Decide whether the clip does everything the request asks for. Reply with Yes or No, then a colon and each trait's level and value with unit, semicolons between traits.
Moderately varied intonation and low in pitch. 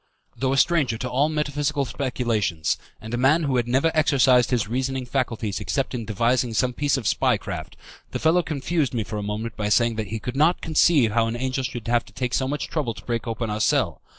Yes: average, 3.4 semitones; low, 125 Hz